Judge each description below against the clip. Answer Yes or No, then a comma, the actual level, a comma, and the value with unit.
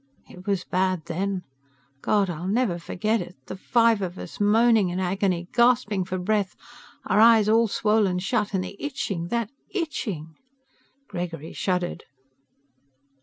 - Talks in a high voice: Yes, high, 195 Hz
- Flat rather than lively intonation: No, average, 3.6 semitones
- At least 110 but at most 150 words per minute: Yes, average, 140 wpm